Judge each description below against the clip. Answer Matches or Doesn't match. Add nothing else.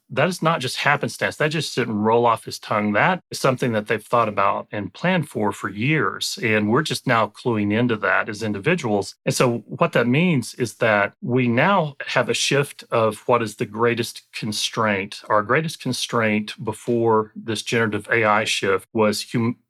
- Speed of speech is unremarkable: Matches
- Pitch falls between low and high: Doesn't match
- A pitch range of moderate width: Matches